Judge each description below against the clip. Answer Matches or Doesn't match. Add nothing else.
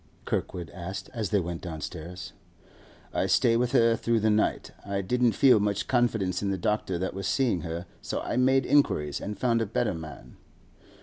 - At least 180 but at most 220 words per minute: Matches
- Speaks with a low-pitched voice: Matches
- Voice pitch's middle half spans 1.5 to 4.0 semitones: Doesn't match